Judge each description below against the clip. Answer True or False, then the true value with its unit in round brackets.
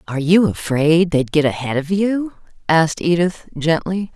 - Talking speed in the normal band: True (160 wpm)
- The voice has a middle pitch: True (165 Hz)